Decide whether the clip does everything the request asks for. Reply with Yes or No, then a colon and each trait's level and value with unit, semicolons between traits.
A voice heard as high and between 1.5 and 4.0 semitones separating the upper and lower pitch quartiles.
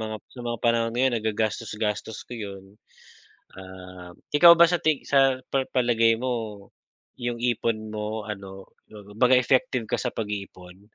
No: low, 110 Hz; average, 3.2 semitones